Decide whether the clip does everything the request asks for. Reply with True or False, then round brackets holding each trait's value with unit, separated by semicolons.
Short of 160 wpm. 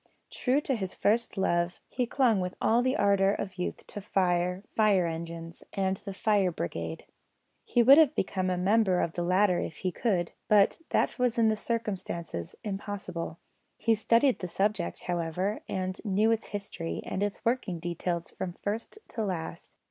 False (170 wpm)